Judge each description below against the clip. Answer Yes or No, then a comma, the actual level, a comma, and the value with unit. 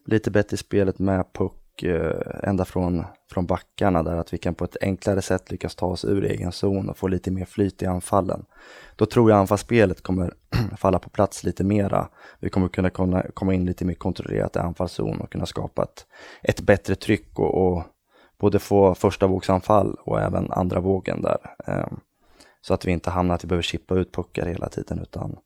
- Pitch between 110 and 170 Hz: No, very low, 95 Hz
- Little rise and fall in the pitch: Yes, narrow, 1.8 semitones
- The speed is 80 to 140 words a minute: No, fast, 195 wpm